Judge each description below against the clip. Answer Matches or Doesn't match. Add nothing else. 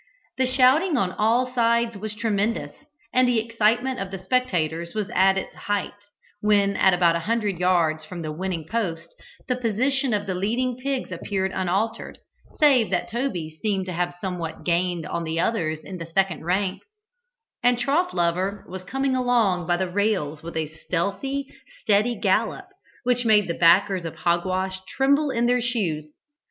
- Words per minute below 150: Doesn't match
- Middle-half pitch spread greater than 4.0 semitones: Matches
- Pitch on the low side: Doesn't match